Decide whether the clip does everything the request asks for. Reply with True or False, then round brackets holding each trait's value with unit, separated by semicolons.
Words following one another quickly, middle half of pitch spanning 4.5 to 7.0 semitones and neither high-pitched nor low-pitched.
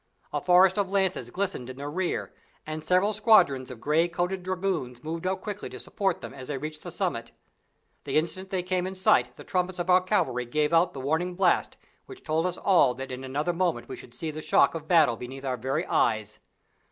True (215 wpm; 5.4 semitones; 170 Hz)